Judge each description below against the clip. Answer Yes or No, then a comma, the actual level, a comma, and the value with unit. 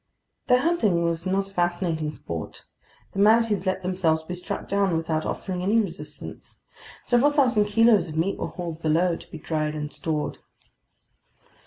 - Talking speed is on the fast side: No, average, 160 wpm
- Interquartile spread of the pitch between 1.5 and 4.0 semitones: No, average, 4.4 semitones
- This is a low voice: No, medium, 180 Hz